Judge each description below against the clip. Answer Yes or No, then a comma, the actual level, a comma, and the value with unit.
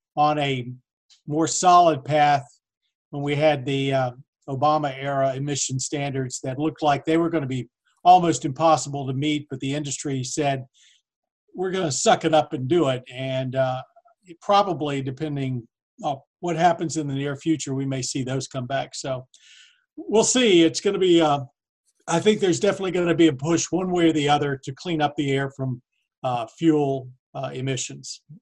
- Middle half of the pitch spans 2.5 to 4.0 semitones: Yes, average, 3.7 semitones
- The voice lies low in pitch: No, medium, 145 Hz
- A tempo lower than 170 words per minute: No, average, 190 wpm